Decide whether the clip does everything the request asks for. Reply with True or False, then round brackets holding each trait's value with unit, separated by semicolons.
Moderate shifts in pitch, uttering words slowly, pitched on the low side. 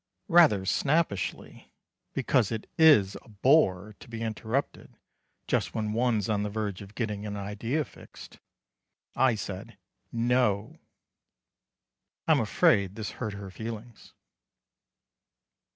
True (3.1 semitones; 115 wpm; 110 Hz)